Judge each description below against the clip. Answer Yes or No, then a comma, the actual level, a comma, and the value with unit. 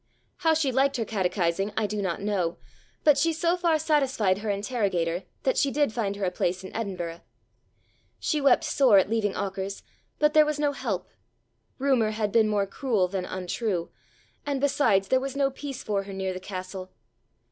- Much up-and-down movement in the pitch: Yes, wide, 6.3 semitones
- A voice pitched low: No, high, 215 Hz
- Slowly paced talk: No, average, 185 wpm